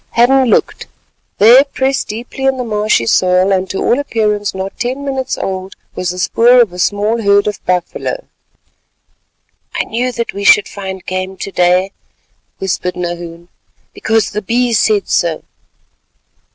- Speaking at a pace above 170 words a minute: No, average, 150 wpm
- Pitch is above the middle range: Yes, high, 205 Hz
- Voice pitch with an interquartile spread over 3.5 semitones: Yes, average, 4.3 semitones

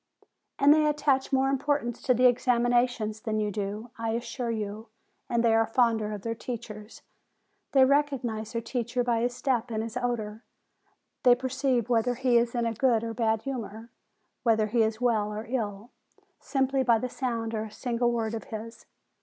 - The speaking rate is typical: Yes, average, 185 wpm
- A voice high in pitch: Yes, high, 235 Hz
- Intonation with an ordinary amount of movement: No, narrow, 2.2 semitones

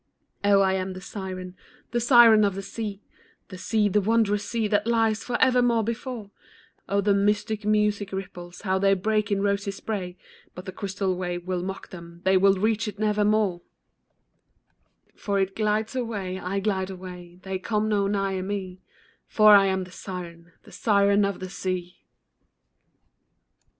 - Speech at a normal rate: Yes, average, 160 wpm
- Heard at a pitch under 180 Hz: No, high, 200 Hz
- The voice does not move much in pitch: Yes, narrow, 2.2 semitones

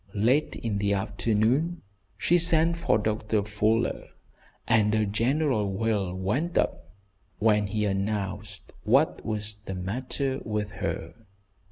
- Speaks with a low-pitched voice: Yes, low, 105 Hz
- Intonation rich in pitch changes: No, average, 3.5 semitones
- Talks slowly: Yes, slow, 125 wpm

